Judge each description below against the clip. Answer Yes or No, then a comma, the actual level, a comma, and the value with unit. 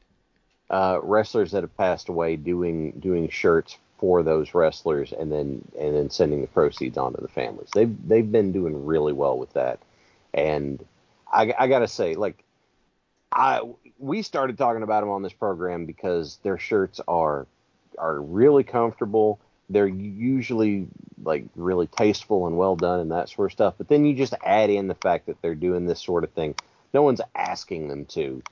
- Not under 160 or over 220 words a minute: Yes, average, 180 wpm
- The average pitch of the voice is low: Yes, very low, 95 Hz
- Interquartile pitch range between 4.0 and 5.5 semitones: Yes, average, 5.1 semitones